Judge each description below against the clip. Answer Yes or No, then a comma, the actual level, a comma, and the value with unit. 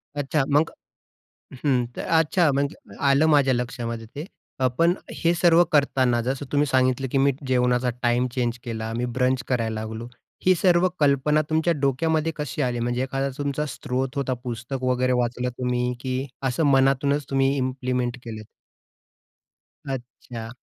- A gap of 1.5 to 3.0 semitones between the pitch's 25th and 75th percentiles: Yes, narrow, 2.6 semitones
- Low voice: Yes, low, 130 Hz